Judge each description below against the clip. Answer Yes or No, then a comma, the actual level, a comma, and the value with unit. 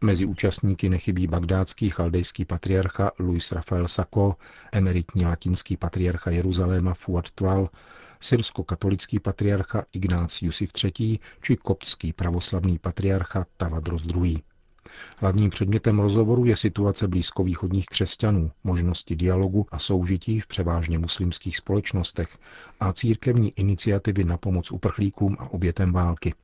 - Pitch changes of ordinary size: No, narrow, 2.2 semitones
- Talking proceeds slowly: Yes, slow, 110 wpm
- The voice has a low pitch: Yes, very low, 95 Hz